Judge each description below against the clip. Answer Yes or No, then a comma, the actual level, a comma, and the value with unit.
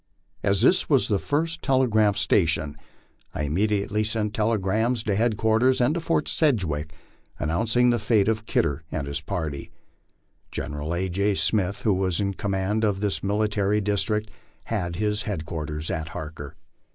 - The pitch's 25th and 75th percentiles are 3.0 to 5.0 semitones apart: Yes, average, 4.3 semitones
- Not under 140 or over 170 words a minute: Yes, average, 155 wpm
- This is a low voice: Yes, low, 105 Hz